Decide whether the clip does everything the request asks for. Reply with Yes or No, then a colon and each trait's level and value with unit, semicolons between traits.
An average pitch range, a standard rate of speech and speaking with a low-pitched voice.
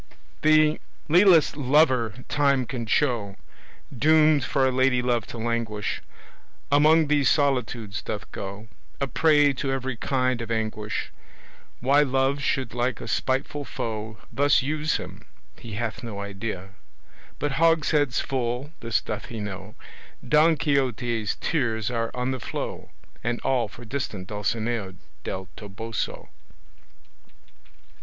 No: average, 4.3 semitones; slow, 130 wpm; low, 125 Hz